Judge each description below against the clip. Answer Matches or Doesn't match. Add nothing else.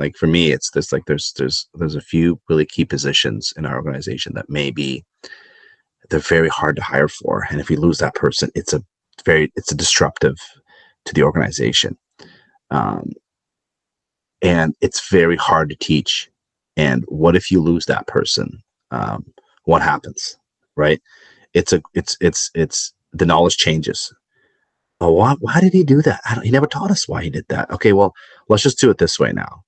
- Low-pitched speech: Matches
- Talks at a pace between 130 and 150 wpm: Doesn't match